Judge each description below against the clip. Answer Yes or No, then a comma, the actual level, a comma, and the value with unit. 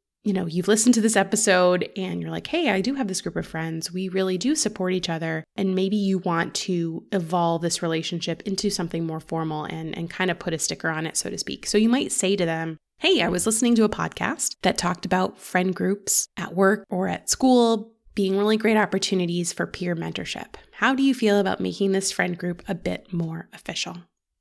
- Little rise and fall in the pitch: No, average, 3.6 semitones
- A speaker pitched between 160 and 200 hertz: Yes, medium, 185 Hz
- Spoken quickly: Yes, fast, 225 wpm